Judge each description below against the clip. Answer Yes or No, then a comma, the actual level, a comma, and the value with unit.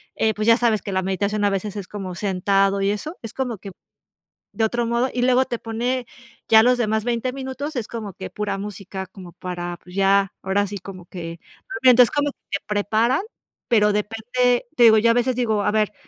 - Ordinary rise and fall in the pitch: Yes, average, 3.4 semitones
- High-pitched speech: Yes, high, 215 Hz